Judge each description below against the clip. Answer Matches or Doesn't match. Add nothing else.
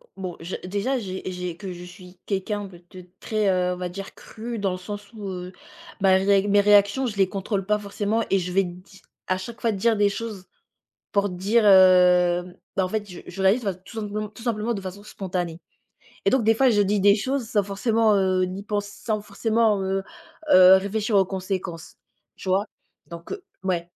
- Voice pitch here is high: Matches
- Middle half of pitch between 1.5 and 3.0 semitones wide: Matches